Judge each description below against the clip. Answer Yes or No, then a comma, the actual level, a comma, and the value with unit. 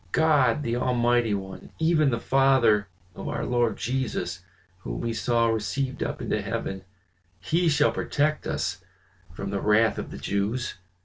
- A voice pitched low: Yes, low, 120 Hz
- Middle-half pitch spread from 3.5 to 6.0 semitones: Yes, average, 4.4 semitones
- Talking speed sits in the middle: Yes, average, 150 wpm